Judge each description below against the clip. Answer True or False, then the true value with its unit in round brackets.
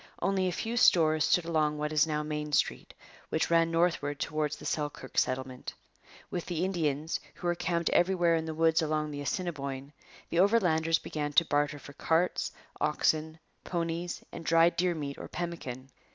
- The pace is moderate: True (170 wpm)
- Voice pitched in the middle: True (160 Hz)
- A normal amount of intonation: False (2.3 semitones)